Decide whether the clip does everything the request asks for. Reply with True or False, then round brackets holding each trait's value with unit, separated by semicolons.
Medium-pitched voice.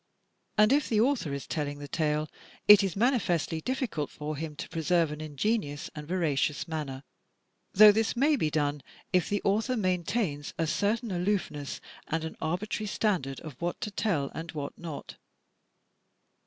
True (170 Hz)